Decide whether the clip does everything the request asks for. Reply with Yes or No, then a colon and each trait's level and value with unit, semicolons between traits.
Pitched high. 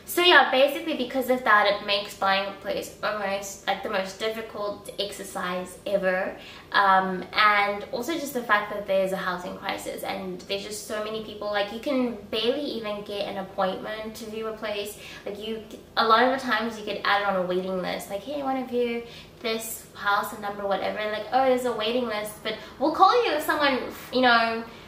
Yes: high, 210 Hz